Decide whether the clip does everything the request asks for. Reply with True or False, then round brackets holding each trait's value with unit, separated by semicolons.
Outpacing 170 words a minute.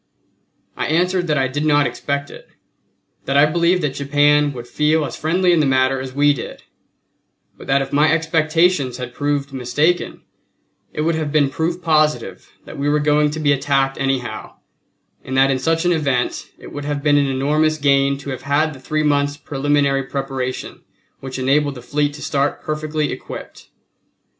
True (180 wpm)